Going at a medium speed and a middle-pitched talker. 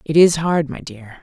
No: fast, 245 wpm; medium, 150 Hz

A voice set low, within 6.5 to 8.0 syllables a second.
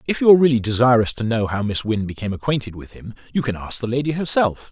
Yes: low, 120 Hz; 6.8 syllables/s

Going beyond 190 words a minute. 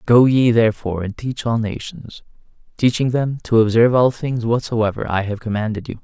No: average, 180 wpm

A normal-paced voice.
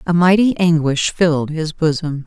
Yes: average, 160 wpm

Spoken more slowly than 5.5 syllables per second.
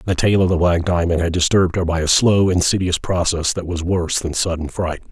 No: 5.8 syllables/s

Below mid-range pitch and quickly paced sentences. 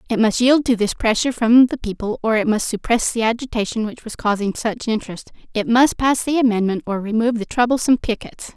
No: high, 225 Hz; fast, 210 wpm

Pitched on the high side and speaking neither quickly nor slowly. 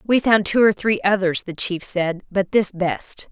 No: high, 195 Hz; fast, 215 wpm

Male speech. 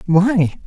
Yes: male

